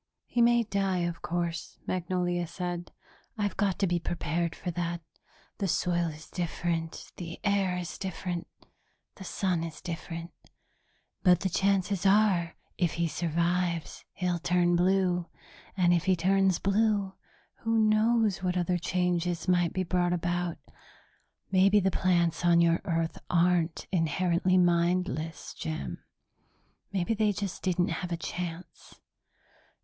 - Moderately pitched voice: Yes, medium, 175 Hz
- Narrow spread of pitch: Yes, narrow, 2.0 semitones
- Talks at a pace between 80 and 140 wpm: Yes, slow, 135 wpm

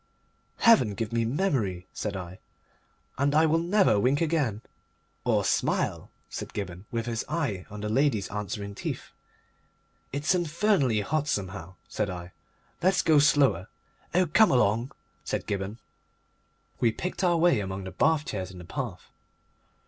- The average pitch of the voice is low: Yes, low, 115 Hz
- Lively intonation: Yes, wide, 7.7 semitones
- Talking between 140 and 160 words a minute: Yes, average, 150 wpm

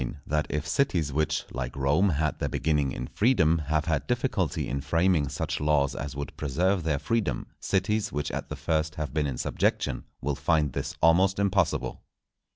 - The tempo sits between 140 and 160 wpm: No, average, 175 wpm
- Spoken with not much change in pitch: No, average, 3.5 semitones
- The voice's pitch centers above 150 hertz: No, very low, 75 Hz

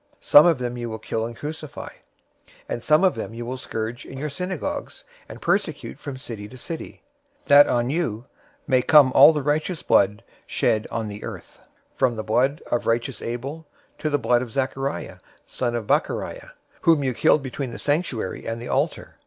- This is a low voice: Yes, low, 130 Hz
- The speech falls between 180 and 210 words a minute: Yes, average, 190 wpm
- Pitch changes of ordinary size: Yes, average, 3.9 semitones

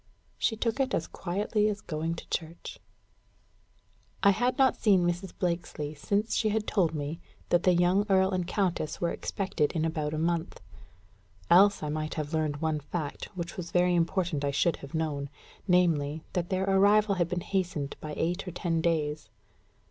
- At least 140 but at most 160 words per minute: No, average, 180 wpm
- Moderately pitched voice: Yes, medium, 175 Hz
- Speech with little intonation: No, average, 3.5 semitones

